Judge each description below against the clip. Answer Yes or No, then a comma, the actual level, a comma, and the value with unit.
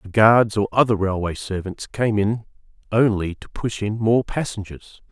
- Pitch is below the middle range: Yes, low, 105 Hz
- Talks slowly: No, average, 165 wpm